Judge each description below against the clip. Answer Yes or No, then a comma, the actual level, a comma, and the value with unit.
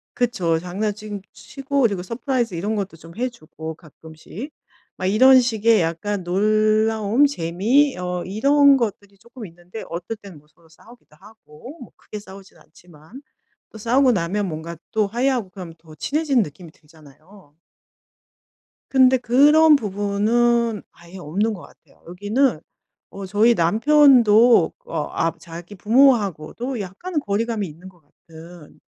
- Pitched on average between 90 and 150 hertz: No, high, 205 Hz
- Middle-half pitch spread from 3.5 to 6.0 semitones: Yes, wide, 5.6 semitones